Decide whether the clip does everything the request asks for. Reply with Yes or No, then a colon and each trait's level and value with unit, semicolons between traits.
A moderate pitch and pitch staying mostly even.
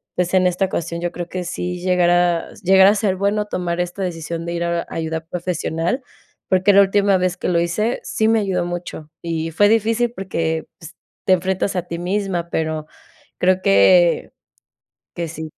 Yes: medium, 180 Hz; narrow, 2.2 semitones